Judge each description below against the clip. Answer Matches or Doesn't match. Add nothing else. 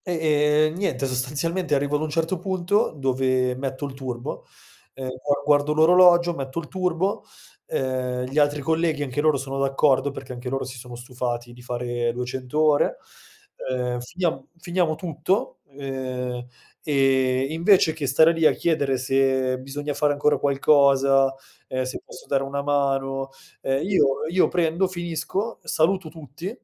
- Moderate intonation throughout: Matches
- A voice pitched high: Doesn't match